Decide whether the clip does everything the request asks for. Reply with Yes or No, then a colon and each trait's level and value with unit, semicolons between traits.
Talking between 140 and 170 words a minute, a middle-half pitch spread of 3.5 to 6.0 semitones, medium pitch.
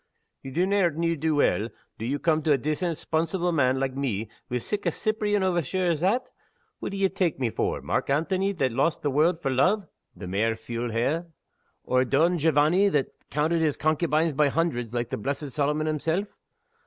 No: average, 190 wpm; average, 4.5 semitones; medium, 155 Hz